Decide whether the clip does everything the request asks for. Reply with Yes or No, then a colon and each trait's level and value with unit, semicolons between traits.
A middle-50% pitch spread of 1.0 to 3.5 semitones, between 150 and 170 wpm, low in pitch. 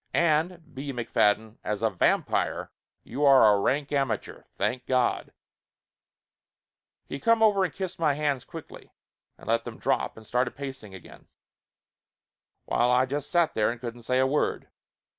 No: average, 3.9 semitones; average, 160 wpm; low, 130 Hz